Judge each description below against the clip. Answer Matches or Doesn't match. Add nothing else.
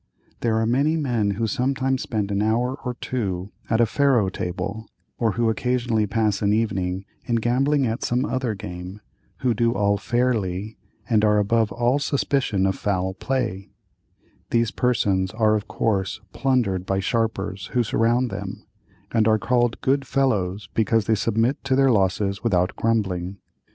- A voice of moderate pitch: Doesn't match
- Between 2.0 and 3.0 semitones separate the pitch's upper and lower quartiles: Doesn't match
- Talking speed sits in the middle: Matches